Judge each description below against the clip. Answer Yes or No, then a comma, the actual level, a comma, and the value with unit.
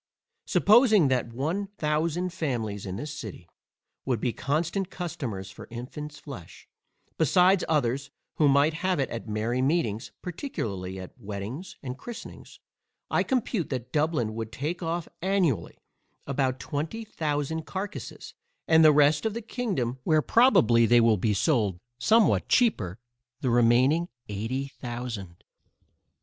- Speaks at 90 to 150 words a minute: Yes, slow, 135 wpm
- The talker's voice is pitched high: No, medium, 140 Hz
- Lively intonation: Yes, wide, 6.5 semitones